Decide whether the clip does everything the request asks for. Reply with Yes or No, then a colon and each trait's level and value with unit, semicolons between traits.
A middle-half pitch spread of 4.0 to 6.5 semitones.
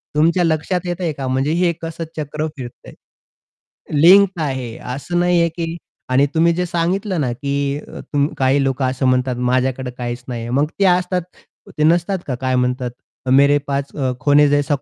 Yes: average, 4.5 semitones